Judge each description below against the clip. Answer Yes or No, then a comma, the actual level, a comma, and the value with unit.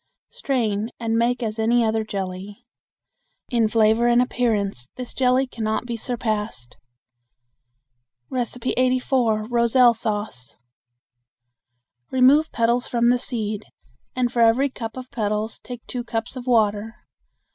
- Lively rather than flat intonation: No, narrow, 2.4 semitones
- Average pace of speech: No, slow, 125 wpm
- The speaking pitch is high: Yes, high, 230 Hz